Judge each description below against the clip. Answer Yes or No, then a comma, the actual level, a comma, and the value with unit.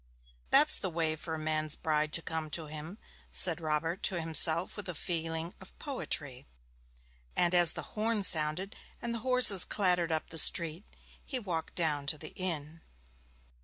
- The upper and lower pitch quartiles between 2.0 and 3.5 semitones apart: Yes, average, 3.0 semitones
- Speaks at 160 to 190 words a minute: Yes, average, 165 wpm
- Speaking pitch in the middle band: Yes, medium, 165 Hz